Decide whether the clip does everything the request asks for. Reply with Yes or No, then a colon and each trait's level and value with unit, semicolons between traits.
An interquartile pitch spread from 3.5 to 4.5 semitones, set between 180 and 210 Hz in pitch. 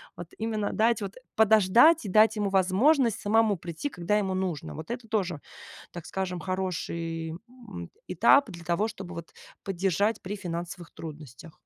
Yes: average, 4.1 semitones; high, 190 Hz